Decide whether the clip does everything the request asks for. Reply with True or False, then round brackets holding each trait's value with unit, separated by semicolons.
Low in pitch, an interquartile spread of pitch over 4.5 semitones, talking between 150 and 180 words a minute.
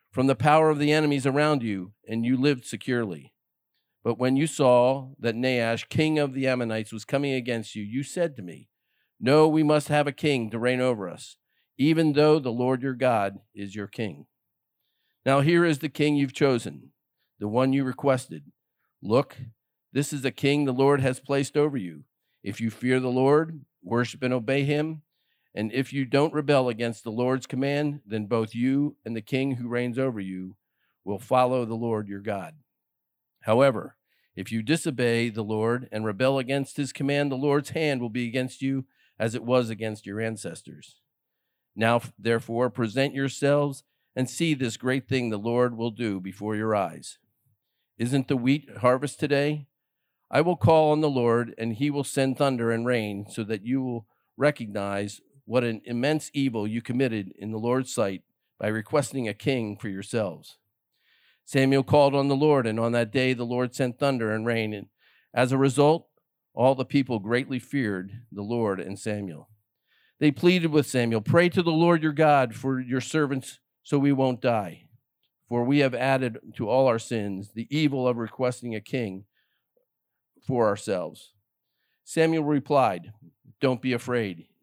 False (130 Hz; 3.8 semitones; 175 wpm)